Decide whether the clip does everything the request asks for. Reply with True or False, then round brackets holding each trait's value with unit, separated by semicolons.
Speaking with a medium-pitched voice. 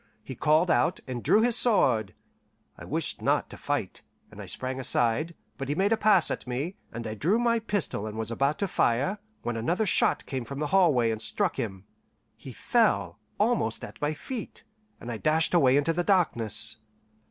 True (145 Hz)